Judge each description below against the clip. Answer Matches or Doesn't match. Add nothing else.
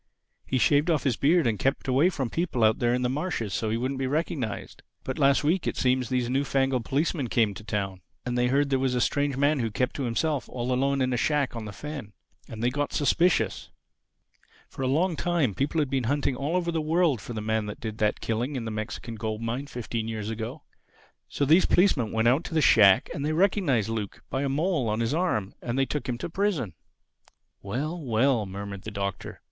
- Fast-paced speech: Matches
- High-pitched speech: Doesn't match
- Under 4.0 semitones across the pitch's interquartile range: Doesn't match